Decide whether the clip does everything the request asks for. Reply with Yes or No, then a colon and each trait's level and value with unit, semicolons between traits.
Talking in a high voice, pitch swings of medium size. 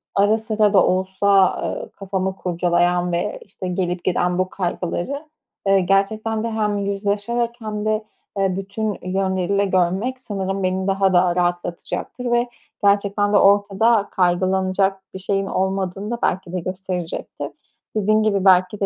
No: high, 195 Hz; narrow, 2.1 semitones